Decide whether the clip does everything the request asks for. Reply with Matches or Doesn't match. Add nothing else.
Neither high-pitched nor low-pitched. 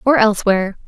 Doesn't match